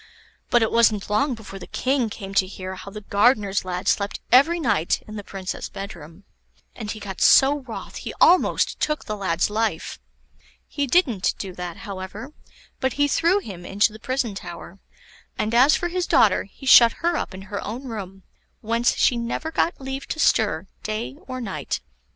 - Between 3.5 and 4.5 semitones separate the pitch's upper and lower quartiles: No, average, 5.2 semitones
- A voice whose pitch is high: Yes, high, 215 Hz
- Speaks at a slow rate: No, average, 185 wpm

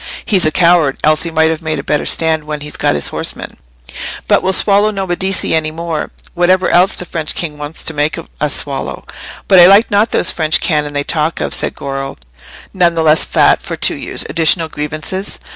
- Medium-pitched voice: Yes, medium, 160 Hz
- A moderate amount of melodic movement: Yes, average, 3.0 semitones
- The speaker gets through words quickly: Yes, fast, 210 wpm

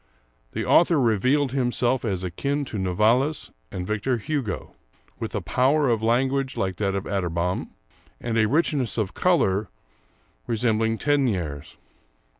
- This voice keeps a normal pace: No, slow, 130 wpm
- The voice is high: No, low, 115 Hz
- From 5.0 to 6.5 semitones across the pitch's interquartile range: Yes, wide, 5.6 semitones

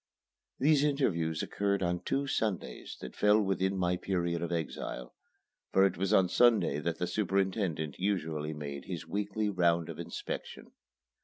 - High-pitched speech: No, very low, 95 Hz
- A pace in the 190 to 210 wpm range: No, average, 150 wpm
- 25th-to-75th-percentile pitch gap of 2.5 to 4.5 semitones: Yes, average, 3.5 semitones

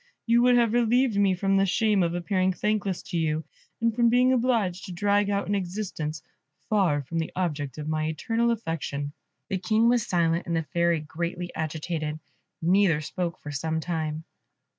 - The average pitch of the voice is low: No, medium, 180 Hz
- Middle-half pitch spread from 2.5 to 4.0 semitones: No, average, 4.8 semitones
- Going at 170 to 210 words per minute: Yes, average, 180 wpm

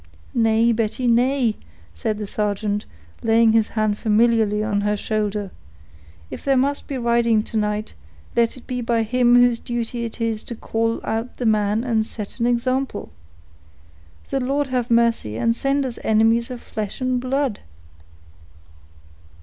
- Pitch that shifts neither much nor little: No, narrow, 2.3 semitones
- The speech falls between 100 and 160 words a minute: Yes, average, 155 wpm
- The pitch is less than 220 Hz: No, high, 230 Hz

